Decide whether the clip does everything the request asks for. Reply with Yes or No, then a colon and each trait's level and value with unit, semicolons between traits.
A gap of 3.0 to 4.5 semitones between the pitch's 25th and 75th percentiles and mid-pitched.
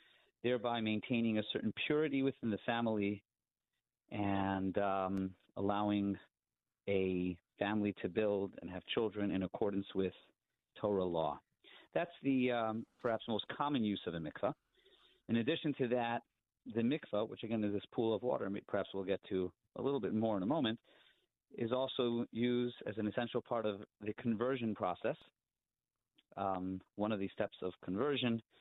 No: average, 3.5 semitones; low, 110 Hz